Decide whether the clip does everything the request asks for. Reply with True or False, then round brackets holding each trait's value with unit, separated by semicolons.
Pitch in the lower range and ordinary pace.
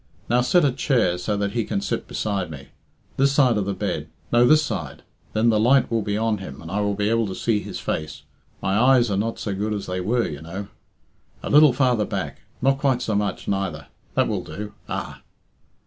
False (105 Hz; 225 wpm)